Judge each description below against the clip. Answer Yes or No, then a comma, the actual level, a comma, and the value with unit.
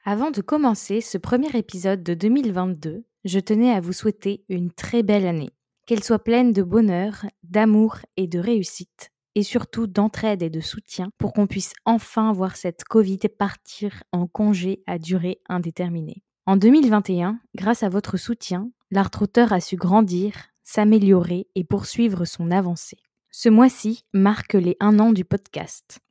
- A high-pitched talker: Yes, high, 205 Hz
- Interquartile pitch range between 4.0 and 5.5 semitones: No, average, 3.0 semitones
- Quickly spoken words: No, average, 155 wpm